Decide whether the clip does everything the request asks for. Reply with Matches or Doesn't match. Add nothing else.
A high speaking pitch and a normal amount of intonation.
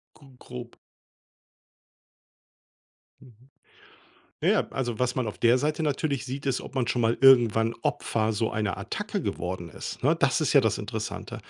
Doesn't match